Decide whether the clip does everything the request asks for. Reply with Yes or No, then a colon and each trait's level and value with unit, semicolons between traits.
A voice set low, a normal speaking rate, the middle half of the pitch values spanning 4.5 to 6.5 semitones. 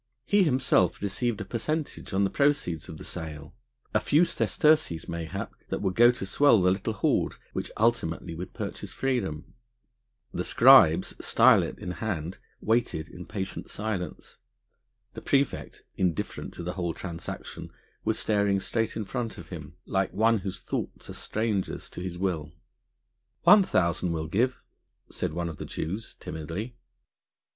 Yes: very low, 95 Hz; average, 150 wpm; average, 5.3 semitones